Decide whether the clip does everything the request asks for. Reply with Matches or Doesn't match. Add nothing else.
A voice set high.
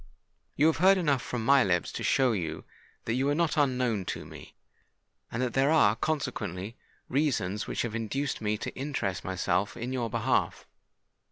Doesn't match